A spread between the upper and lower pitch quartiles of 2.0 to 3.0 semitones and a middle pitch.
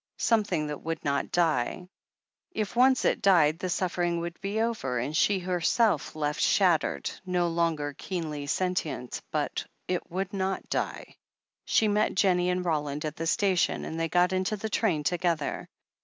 No: average, 3.6 semitones; medium, 175 Hz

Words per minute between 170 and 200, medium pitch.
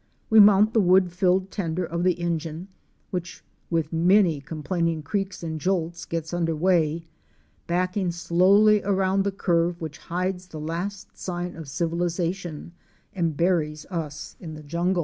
No: average, 150 wpm; medium, 175 Hz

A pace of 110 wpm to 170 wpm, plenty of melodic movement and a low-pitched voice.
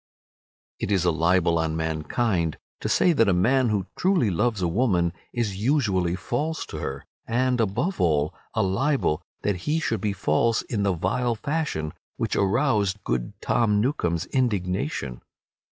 Yes: average, 155 wpm; wide, 6.1 semitones; low, 100 Hz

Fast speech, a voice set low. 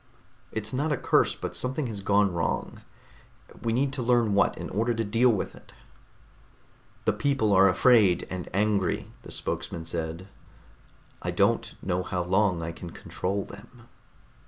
No: average, 160 wpm; low, 105 Hz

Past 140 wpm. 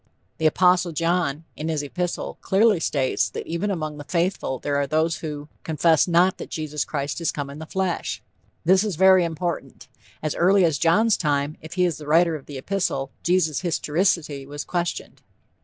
Yes: average, 185 wpm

